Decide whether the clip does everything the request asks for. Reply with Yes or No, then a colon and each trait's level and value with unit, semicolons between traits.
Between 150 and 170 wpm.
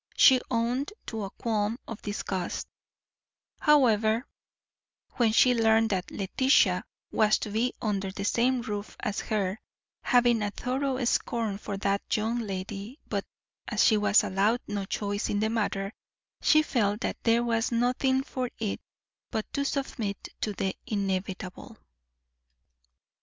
No: average, 140 wpm